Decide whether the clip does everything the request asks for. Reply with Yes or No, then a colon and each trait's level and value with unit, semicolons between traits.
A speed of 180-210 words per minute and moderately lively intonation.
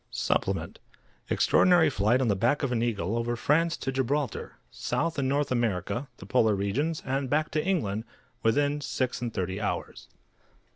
No: average, 160 wpm; average, 4.7 semitones